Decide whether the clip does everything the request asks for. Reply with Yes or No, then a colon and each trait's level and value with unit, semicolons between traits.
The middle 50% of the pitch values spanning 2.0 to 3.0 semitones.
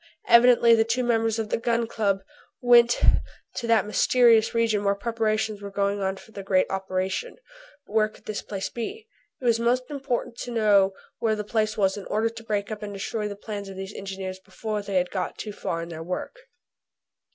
Yes: average, 2.7 semitones